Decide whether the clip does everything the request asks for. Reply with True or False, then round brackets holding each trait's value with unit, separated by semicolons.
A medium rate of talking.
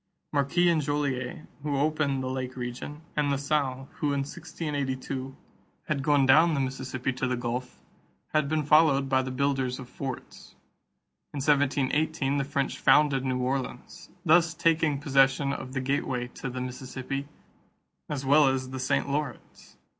True (155 wpm)